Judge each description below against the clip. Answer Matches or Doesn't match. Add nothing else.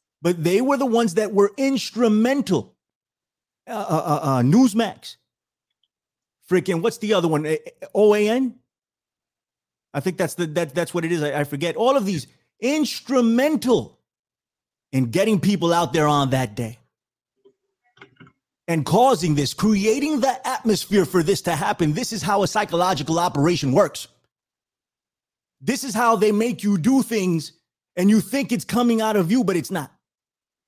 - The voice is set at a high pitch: Matches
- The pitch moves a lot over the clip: Matches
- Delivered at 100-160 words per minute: Matches